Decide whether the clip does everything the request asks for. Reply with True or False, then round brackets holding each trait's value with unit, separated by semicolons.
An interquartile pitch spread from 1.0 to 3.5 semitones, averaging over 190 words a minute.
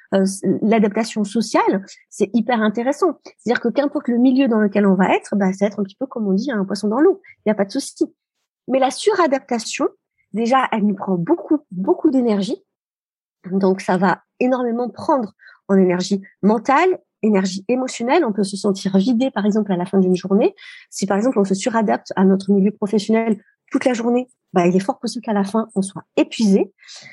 False (5.1 semitones; 205 wpm)